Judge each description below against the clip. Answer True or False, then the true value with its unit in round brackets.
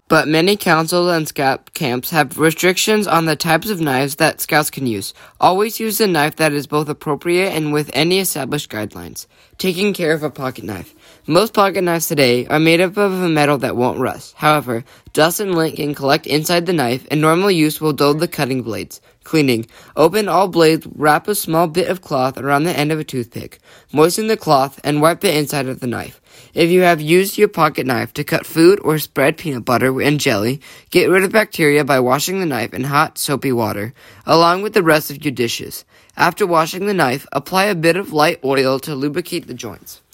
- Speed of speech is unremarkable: False (210 wpm)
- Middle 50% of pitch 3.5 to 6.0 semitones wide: True (4.2 semitones)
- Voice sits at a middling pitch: True (155 Hz)